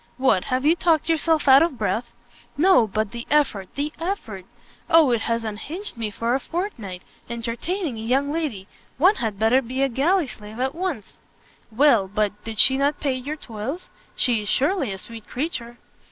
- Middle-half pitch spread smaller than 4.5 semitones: No, wide, 5.5 semitones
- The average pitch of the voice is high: Yes, very high, 255 Hz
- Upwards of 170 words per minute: Yes, average, 180 wpm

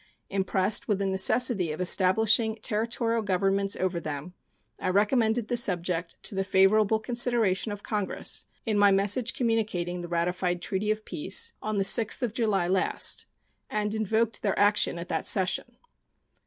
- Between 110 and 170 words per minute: Yes, average, 155 wpm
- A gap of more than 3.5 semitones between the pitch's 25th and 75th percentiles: No, average, 3.1 semitones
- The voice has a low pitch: No, high, 205 Hz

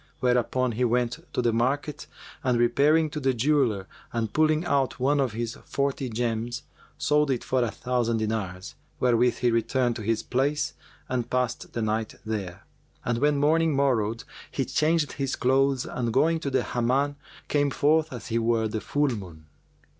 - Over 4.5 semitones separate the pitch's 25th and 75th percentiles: No, average, 3.6 semitones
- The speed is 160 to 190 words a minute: Yes, average, 170 wpm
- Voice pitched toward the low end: Yes, low, 125 Hz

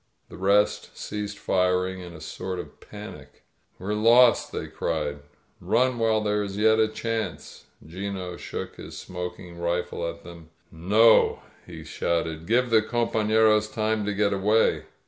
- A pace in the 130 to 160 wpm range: Yes, average, 145 wpm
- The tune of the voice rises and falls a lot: No, average, 3.7 semitones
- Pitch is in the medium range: No, low, 100 Hz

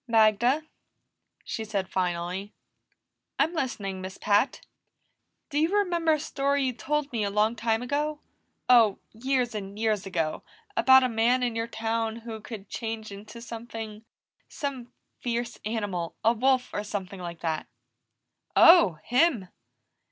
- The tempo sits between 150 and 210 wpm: No, average, 140 wpm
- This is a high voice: Yes, high, 225 Hz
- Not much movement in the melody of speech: No, average, 3.9 semitones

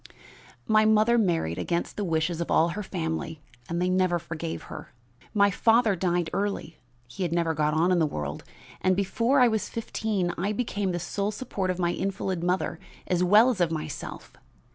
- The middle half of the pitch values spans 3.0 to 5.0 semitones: Yes, average, 3.6 semitones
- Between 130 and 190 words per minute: Yes, average, 185 wpm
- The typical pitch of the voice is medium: Yes, medium, 180 Hz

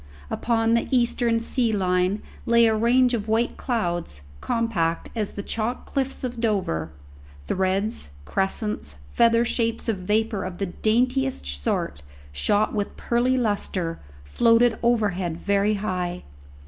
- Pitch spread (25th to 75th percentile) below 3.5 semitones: No, average, 4.1 semitones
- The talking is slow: Yes, slow, 130 wpm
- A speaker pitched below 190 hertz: No, high, 215 Hz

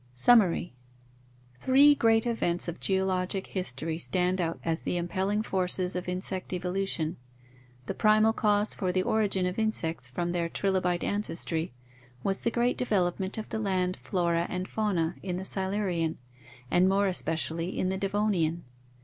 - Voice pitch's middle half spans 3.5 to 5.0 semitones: No, average, 2.9 semitones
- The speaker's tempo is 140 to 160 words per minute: Yes, average, 150 wpm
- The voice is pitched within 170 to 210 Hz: Yes, medium, 185 Hz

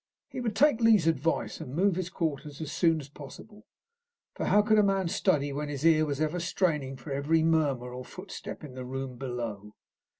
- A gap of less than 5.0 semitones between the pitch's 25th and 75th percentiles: No, average, 5.3 semitones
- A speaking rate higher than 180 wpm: Yes, average, 200 wpm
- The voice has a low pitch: No, medium, 155 Hz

